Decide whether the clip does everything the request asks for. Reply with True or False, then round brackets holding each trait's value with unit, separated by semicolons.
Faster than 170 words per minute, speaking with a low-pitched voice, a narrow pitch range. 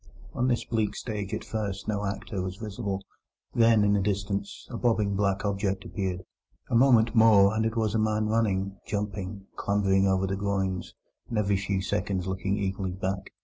True (180 wpm; 100 Hz; 2.0 semitones)